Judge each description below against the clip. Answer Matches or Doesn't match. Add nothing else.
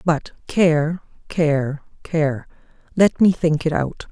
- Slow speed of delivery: Matches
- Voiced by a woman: Matches